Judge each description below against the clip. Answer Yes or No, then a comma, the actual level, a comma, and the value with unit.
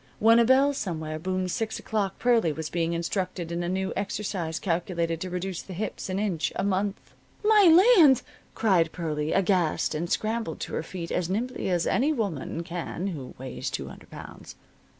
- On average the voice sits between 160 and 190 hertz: Yes, medium, 185 Hz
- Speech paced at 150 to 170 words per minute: No, average, 180 wpm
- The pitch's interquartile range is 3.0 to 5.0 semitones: Yes, average, 4.3 semitones